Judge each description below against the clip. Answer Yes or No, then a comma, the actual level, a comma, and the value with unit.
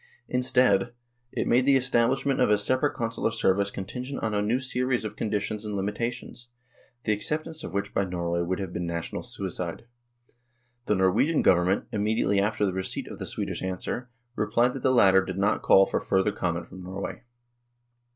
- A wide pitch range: No, average, 4.5 semitones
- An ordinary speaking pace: Yes, average, 180 wpm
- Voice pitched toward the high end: No, low, 105 Hz